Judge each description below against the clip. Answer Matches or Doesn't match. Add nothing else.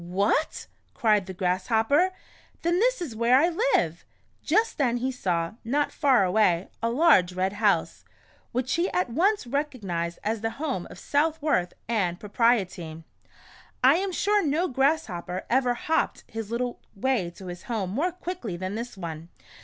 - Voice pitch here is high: Matches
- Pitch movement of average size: Doesn't match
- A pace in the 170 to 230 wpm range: Doesn't match